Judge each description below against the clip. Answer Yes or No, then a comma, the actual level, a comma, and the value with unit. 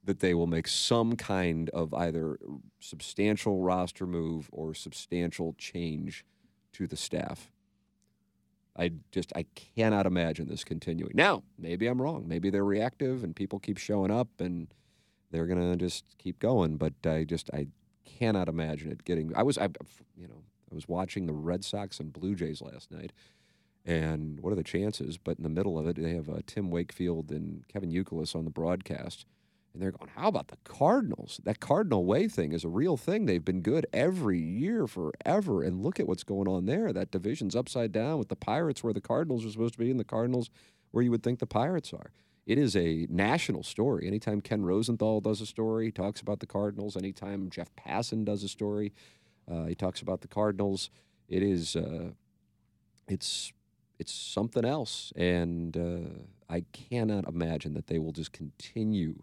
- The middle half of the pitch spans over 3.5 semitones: Yes, average, 4.2 semitones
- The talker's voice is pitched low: Yes, very low, 95 Hz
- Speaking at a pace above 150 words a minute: Yes, average, 190 wpm